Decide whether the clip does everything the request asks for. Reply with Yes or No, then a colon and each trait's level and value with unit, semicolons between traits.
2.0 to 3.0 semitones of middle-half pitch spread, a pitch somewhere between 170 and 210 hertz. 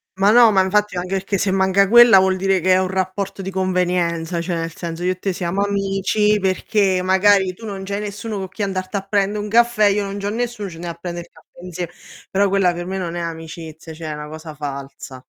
Yes: narrow, 2.5 semitones; high, 190 Hz